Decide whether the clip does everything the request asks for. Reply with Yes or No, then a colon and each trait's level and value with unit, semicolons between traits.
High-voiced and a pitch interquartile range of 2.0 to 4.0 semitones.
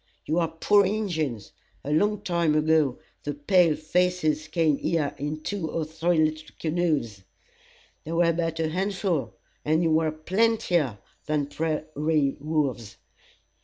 No: medium, 160 Hz; narrow, 2.4 semitones